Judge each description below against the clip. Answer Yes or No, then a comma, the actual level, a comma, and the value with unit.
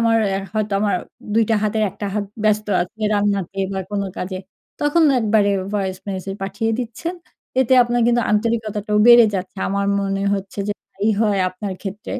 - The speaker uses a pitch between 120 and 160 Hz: No, high, 210 Hz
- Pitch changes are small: Yes, narrow, 2.3 semitones